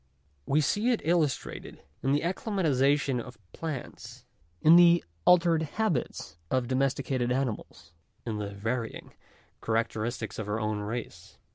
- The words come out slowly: Yes, slow, 130 wpm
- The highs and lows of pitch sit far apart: Yes, wide, 6.2 semitones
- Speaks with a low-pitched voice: Yes, low, 130 Hz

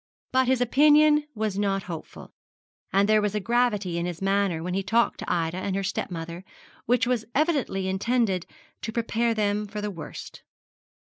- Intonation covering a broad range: No, average, 4.1 semitones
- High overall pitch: Yes, high, 210 Hz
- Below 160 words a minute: No, average, 175 wpm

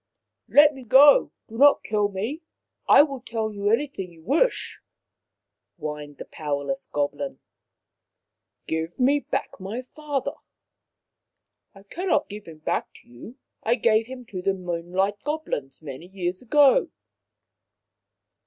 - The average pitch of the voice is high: Yes, high, 210 Hz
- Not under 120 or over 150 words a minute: Yes, average, 140 wpm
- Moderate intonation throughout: No, wide, 7.7 semitones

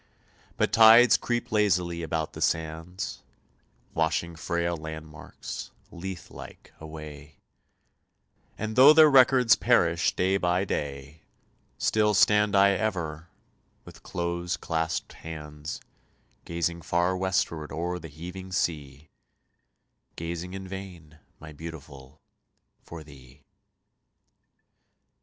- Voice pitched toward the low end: Yes, very low, 85 Hz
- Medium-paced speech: No, slow, 100 wpm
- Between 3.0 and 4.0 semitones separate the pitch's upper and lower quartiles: Yes, average, 3.4 semitones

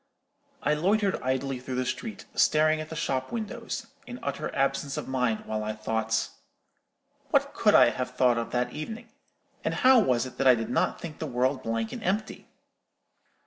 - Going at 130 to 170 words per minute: No, average, 185 wpm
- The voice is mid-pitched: No, low, 130 Hz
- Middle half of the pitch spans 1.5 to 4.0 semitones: No, average, 4.6 semitones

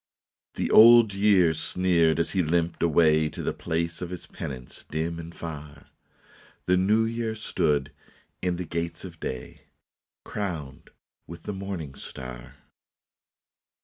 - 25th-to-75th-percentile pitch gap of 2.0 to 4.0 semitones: Yes, average, 3.2 semitones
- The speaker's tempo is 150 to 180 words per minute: No, average, 140 wpm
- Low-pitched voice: Yes, very low, 85 Hz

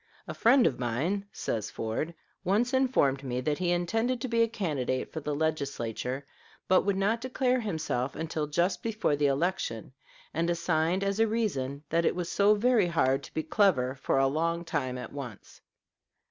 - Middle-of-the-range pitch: Yes, medium, 165 Hz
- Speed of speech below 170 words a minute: No, average, 180 wpm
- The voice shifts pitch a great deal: Yes, wide, 6.9 semitones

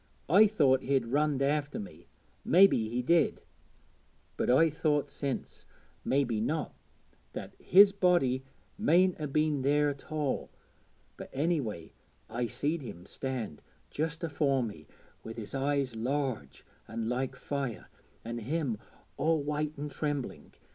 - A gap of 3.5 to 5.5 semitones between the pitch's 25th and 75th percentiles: Yes, average, 3.9 semitones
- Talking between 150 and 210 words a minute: No, slow, 135 wpm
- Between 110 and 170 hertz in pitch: Yes, medium, 140 Hz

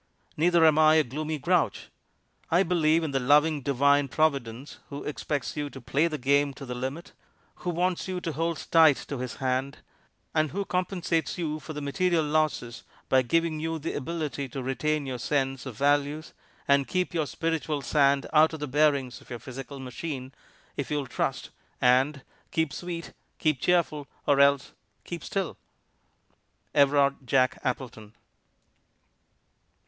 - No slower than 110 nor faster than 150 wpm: No, average, 160 wpm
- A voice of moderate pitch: Yes, medium, 145 Hz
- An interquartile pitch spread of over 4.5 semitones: No, average, 3.1 semitones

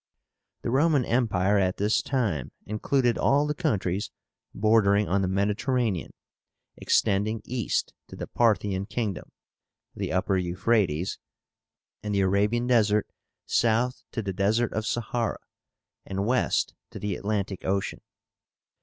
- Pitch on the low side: Yes, low, 105 Hz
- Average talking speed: No, slow, 125 wpm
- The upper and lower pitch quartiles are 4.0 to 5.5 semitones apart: No, average, 3.3 semitones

